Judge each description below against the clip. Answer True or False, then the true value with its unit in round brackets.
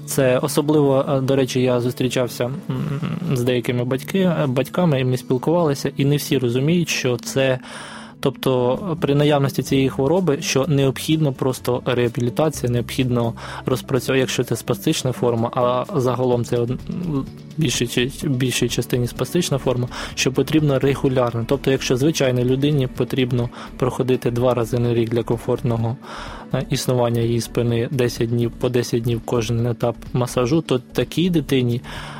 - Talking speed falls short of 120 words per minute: False (135 wpm)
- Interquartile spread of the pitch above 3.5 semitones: False (2.4 semitones)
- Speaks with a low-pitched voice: True (130 Hz)